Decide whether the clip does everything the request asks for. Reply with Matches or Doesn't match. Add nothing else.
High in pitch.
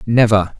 Doesn't match